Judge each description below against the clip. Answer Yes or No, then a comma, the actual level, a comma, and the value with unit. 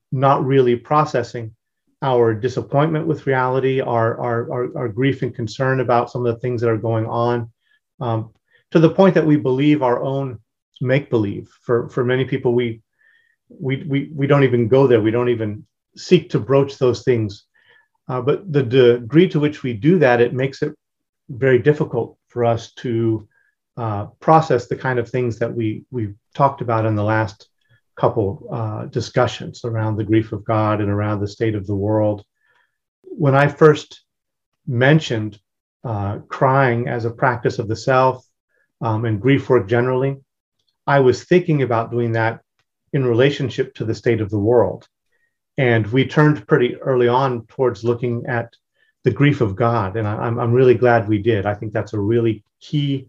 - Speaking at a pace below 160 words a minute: No, average, 175 wpm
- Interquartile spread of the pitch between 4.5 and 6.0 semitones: No, average, 3.2 semitones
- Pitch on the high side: No, low, 125 Hz